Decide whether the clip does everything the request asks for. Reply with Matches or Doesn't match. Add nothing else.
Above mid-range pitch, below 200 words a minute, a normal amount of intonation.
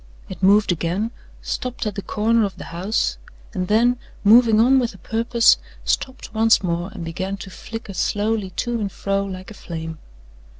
Matches